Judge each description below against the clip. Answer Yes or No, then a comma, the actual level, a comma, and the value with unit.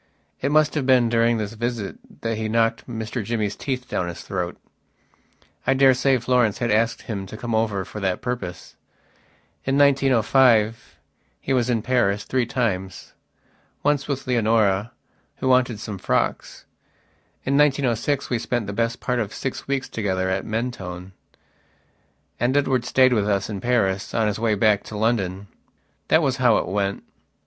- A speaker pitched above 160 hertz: No, low, 115 Hz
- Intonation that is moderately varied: Yes, average, 3.7 semitones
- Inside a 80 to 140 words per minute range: No, average, 160 wpm